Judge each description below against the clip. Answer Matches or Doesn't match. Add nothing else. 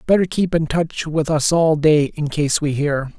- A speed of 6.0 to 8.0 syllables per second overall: Doesn't match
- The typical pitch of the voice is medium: Matches